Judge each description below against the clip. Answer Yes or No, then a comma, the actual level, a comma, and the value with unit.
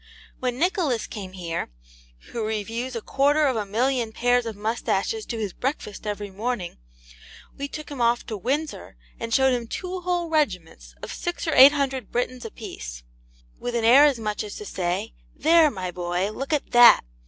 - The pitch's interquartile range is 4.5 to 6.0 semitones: Yes, average, 5.0 semitones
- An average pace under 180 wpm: No, average, 190 wpm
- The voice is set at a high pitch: Yes, high, 235 Hz